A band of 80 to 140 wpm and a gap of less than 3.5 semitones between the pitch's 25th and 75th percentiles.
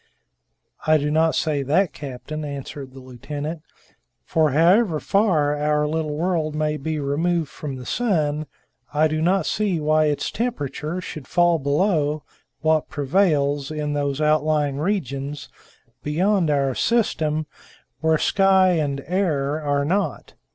Yes: slow, 135 wpm; average, 2.7 semitones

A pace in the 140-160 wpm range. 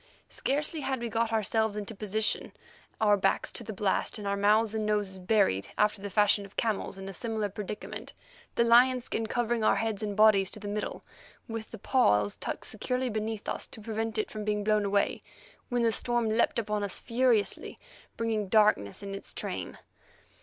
No: average, 190 wpm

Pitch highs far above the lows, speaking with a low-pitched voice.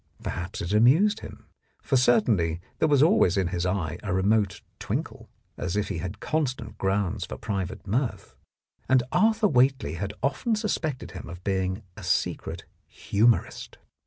Yes: wide, 6.5 semitones; low, 105 Hz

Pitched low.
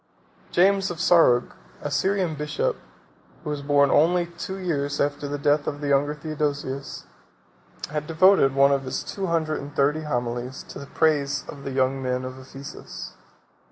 No: medium, 145 Hz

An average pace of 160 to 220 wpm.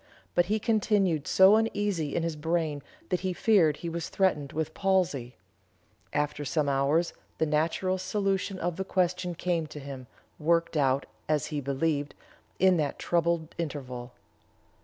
No: average, 150 wpm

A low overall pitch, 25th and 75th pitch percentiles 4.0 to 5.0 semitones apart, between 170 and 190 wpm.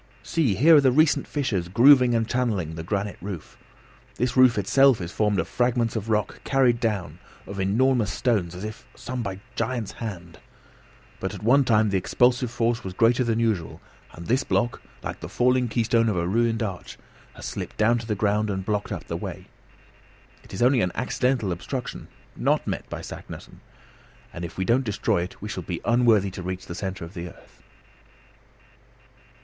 Yes: low, 110 Hz; average, 4.4 semitones; average, 185 wpm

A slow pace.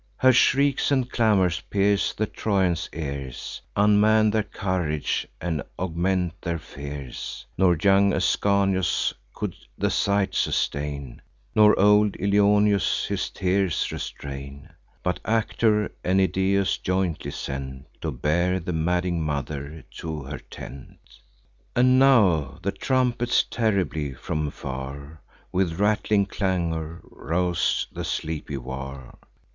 Yes: slow, 115 wpm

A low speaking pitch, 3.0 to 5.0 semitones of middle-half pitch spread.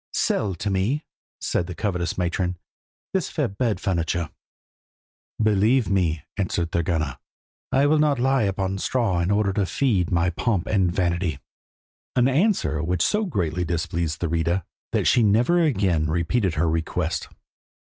Yes: very low, 95 Hz; average, 4.6 semitones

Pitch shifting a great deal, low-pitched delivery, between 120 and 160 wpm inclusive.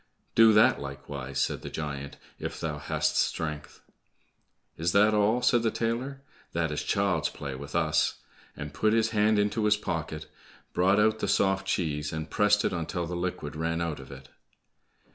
No: wide, 6.1 semitones; very low, 85 Hz; average, 175 wpm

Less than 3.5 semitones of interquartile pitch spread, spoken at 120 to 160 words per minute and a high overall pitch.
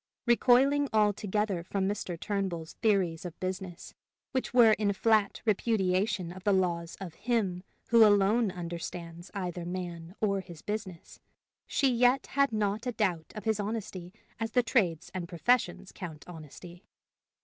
No: average, 3.9 semitones; average, 145 wpm; high, 195 Hz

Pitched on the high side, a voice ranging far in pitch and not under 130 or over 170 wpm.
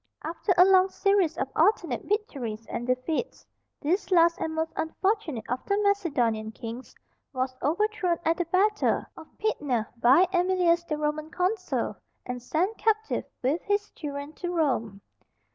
Yes: very high, 330 Hz; wide, 6.3 semitones; average, 145 wpm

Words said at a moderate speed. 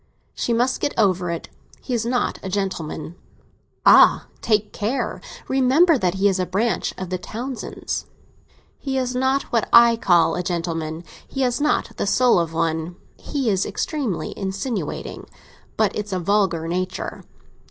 Yes: average, 155 wpm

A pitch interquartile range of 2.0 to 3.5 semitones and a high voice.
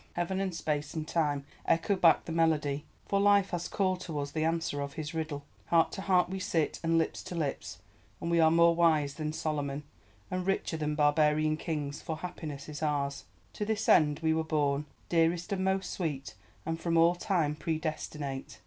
No: narrow, 2.6 semitones; medium, 160 Hz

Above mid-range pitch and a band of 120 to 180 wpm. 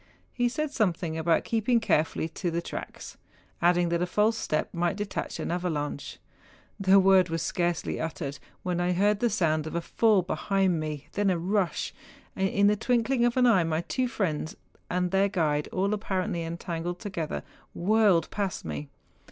No: medium, 180 Hz; average, 170 wpm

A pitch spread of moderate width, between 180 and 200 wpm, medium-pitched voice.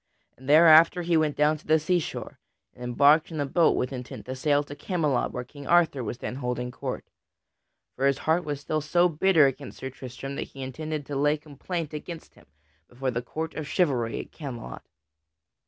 Yes: average, 3.3 semitones; average, 195 wpm; medium, 145 Hz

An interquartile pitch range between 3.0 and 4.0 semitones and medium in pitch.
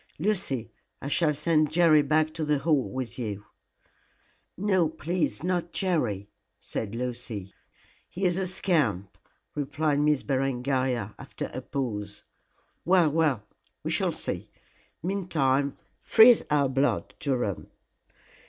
No: average, 5.2 semitones; medium, 145 Hz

